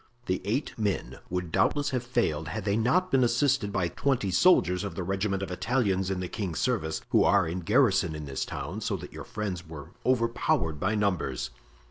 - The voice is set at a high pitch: No, low, 100 Hz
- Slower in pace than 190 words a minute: No, average, 195 wpm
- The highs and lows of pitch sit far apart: No, average, 4.9 semitones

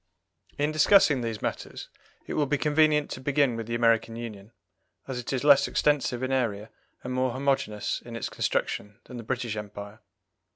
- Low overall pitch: Yes, low, 125 Hz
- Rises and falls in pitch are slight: No, average, 3.8 semitones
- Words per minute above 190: No, average, 175 wpm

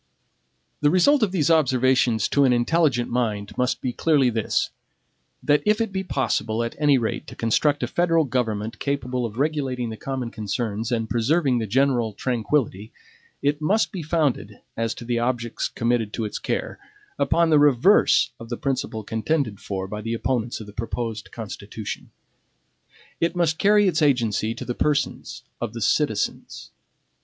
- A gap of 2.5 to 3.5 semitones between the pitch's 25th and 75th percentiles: No, average, 4.8 semitones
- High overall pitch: No, low, 125 Hz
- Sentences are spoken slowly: No, average, 165 wpm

